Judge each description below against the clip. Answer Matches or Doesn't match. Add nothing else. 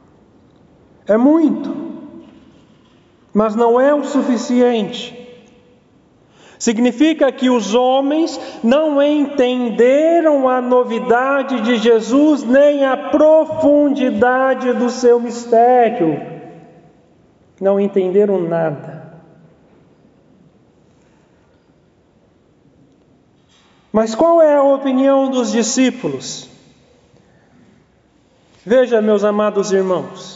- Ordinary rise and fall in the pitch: Matches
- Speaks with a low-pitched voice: Doesn't match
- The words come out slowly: Matches